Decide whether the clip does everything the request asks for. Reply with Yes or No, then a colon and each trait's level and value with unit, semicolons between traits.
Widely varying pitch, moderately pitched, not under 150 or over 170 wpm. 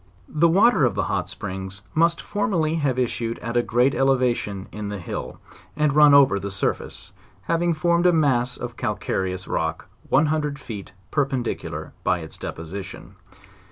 No: wide, 7.1 semitones; low, 130 Hz; average, 160 wpm